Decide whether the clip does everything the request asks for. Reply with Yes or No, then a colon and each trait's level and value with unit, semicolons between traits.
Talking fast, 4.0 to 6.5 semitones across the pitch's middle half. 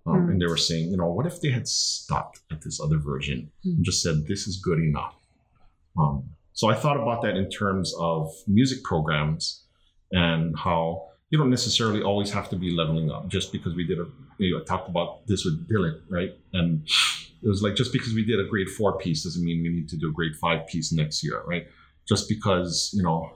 Yes: fast, 225 wpm; average, 4.4 semitones